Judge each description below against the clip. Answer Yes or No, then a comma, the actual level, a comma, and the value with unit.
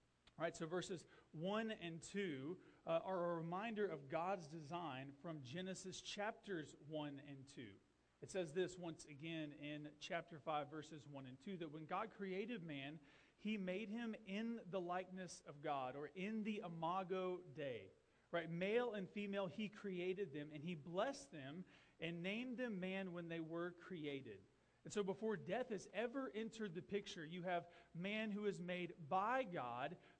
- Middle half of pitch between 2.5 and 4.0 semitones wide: Yes, average, 3.7 semitones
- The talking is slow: No, average, 170 wpm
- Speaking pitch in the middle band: Yes, medium, 180 Hz